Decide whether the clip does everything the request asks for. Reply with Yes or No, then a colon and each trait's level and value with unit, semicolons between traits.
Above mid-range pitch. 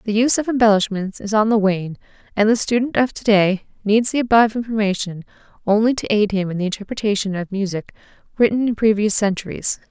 Yes: high, 210 Hz